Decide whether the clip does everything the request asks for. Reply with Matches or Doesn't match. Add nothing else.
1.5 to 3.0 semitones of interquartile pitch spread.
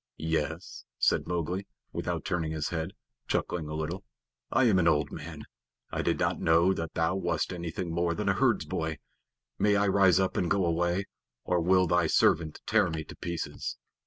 Matches